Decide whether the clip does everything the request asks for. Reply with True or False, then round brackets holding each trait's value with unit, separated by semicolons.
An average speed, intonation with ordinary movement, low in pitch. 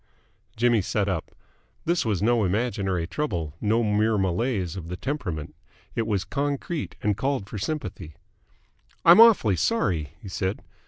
True (145 wpm; 5.0 semitones; 105 Hz)